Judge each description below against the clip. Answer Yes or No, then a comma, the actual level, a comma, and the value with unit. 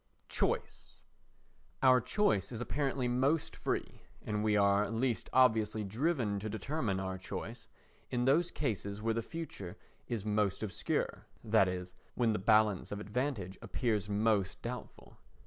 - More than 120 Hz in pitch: No, low, 110 Hz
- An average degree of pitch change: Yes, average, 3.6 semitones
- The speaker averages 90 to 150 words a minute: Yes, average, 140 wpm